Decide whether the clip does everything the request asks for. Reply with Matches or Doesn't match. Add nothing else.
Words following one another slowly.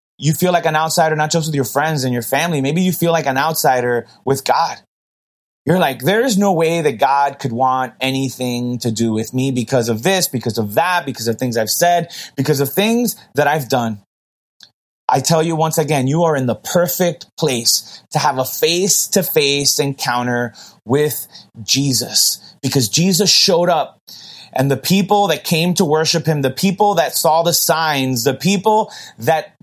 Doesn't match